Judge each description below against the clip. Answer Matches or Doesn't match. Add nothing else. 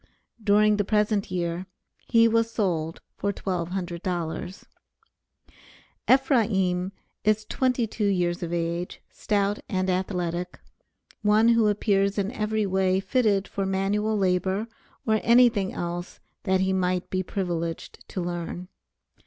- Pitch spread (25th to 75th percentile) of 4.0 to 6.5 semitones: Doesn't match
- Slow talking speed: Matches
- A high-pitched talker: Matches